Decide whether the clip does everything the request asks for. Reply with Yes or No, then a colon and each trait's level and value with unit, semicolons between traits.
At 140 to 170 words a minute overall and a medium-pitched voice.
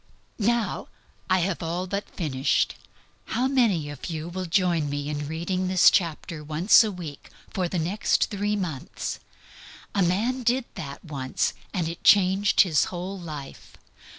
Yes: average, 150 wpm; medium, 180 Hz